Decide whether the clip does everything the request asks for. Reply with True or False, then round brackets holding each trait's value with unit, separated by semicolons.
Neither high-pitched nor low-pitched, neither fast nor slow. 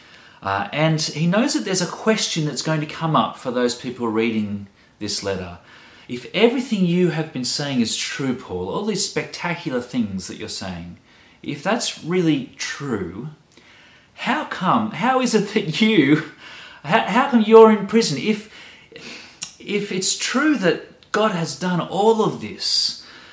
True (160 Hz; 160 wpm)